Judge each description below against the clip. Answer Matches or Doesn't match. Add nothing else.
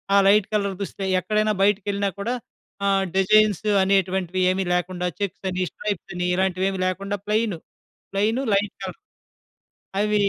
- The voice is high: Matches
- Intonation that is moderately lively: Doesn't match